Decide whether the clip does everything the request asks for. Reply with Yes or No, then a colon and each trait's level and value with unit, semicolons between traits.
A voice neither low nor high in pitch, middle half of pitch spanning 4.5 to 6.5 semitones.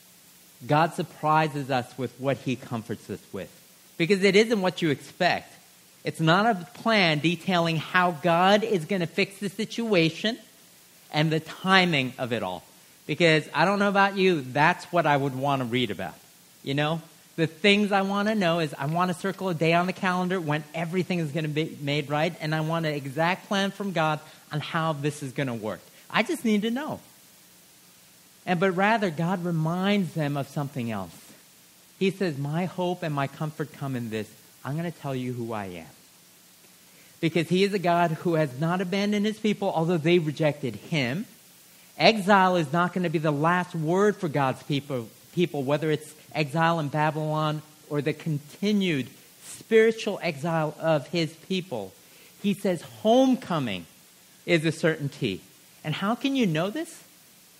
No: medium, 165 Hz; average, 4.0 semitones